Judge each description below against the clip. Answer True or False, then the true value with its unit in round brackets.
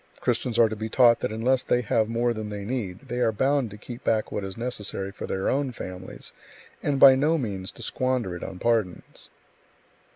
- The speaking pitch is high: False (115 Hz)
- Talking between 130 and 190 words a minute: False (205 wpm)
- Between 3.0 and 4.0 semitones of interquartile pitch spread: True (3.6 semitones)